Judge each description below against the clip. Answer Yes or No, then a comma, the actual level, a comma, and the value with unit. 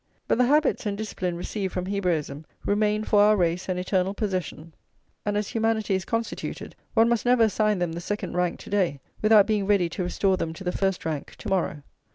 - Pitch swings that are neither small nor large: Yes, average, 3.1 semitones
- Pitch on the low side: No, high, 195 Hz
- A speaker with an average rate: No, fast, 210 wpm